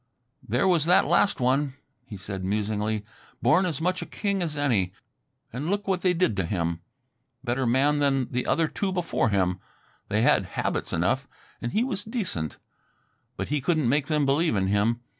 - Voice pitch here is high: No, low, 135 Hz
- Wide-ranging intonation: Yes, wide, 8.4 semitones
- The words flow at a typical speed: Yes, average, 180 wpm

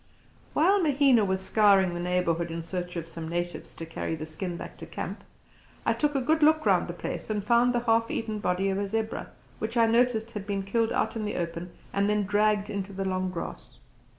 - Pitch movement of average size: Yes, average, 4.1 semitones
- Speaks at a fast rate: Yes, fast, 220 wpm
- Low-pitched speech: No, high, 205 Hz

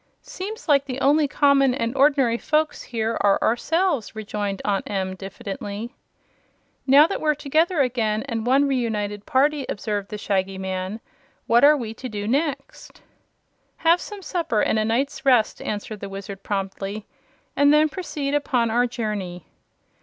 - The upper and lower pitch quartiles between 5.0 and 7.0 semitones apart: Yes, wide, 5.5 semitones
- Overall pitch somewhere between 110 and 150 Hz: No, high, 235 Hz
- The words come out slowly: No, average, 155 wpm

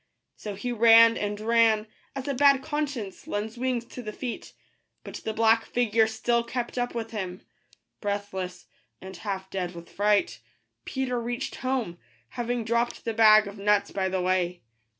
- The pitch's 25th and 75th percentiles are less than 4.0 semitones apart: Yes, average, 3.1 semitones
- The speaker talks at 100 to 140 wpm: No, average, 165 wpm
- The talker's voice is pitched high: Yes, high, 225 Hz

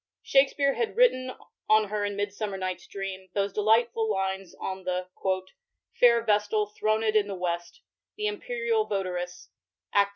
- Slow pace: No, average, 150 wpm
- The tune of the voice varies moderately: Yes, average, 3.6 semitones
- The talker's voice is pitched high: Yes, high, 210 Hz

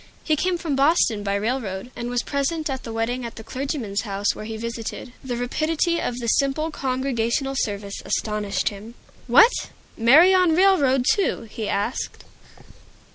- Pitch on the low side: No, very high, 250 Hz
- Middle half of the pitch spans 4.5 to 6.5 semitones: Yes, average, 5.3 semitones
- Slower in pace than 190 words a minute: Yes, average, 160 wpm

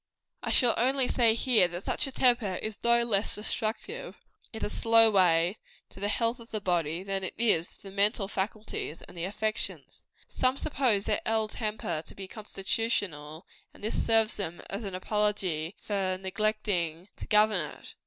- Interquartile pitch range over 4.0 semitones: No, average, 3.3 semitones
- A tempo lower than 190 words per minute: Yes, average, 175 wpm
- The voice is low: No, high, 210 Hz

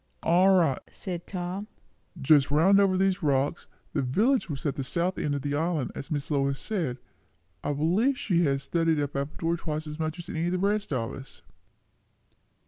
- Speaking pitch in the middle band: Yes, medium, 160 Hz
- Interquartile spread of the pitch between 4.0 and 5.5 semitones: Yes, average, 4.5 semitones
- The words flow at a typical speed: Yes, average, 190 wpm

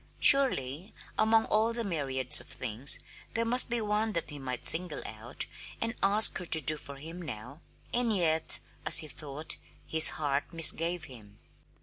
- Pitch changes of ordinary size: No, wide, 7.5 semitones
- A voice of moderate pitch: Yes, medium, 160 Hz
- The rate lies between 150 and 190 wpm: Yes, average, 160 wpm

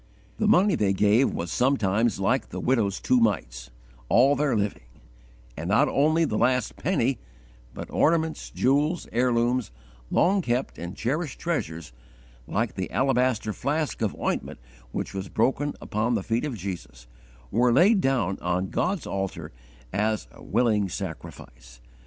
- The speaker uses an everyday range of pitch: No, wide, 6.0 semitones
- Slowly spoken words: No, average, 145 wpm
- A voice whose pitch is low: Yes, low, 120 Hz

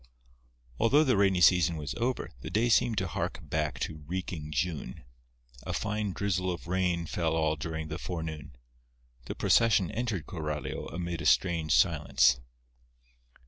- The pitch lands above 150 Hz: No, very low, 85 Hz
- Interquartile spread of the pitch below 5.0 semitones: Yes, average, 3.9 semitones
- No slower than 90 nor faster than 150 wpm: Yes, average, 145 wpm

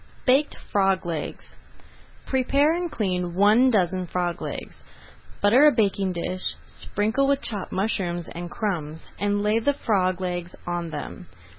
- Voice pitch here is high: Yes, high, 195 Hz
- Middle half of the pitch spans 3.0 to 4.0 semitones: No, average, 4.4 semitones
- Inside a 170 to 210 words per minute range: No, average, 140 wpm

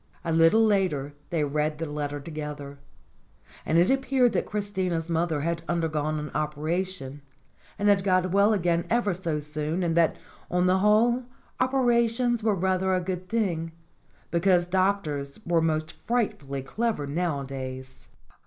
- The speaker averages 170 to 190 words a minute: No, average, 145 wpm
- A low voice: No, medium, 170 Hz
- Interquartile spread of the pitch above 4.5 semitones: Yes, average, 4.9 semitones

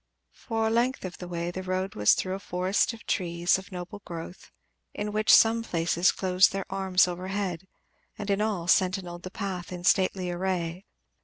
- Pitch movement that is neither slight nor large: No, narrow, 2.0 semitones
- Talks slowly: No, average, 175 wpm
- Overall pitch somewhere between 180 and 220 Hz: Yes, medium, 185 Hz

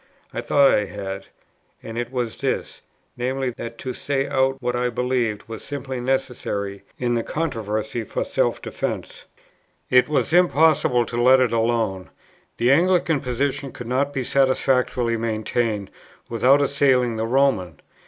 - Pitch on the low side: Yes, low, 125 Hz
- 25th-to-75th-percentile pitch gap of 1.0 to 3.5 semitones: Yes, average, 2.9 semitones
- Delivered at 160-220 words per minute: No, average, 145 wpm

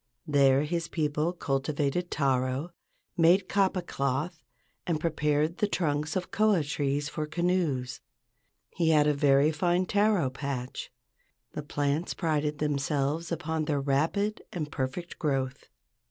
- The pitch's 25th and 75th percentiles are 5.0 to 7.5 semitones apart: No, average, 3.5 semitones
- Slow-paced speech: Yes, slow, 125 wpm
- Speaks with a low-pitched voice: No, medium, 150 Hz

